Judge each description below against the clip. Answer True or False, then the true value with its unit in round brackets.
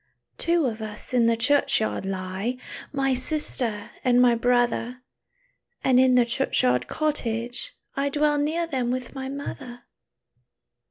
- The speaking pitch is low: False (250 Hz)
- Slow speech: True (130 wpm)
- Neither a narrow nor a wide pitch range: True (3.2 semitones)